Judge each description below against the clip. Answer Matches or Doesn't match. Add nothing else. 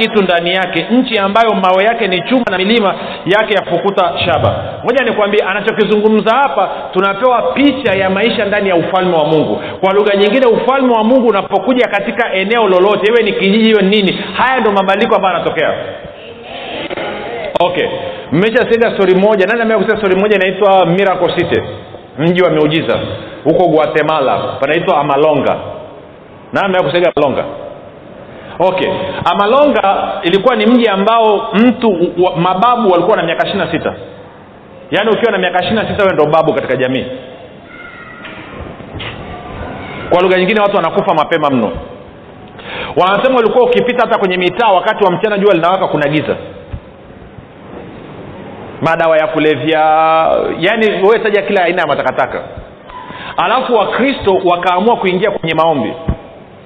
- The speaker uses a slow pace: Doesn't match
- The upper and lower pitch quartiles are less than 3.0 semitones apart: Doesn't match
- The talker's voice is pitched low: Doesn't match